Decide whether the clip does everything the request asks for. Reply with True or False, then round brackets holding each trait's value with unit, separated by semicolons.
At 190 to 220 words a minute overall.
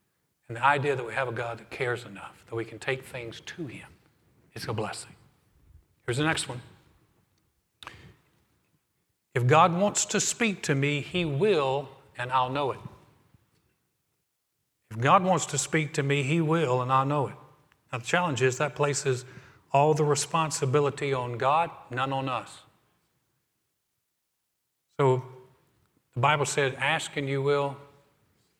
False (155 wpm)